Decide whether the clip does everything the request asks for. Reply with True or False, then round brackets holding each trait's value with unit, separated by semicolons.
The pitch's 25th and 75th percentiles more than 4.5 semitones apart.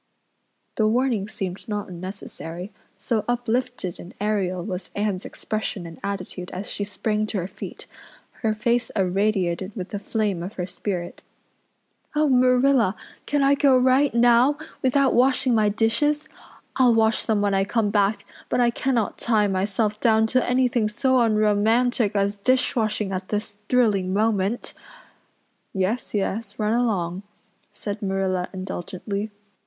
False (3.8 semitones)